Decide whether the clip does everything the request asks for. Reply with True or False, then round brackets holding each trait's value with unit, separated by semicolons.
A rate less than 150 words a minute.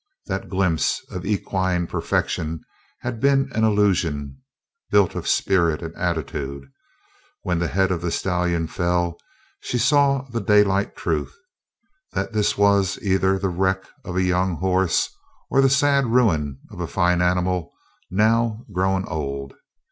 True (140 wpm)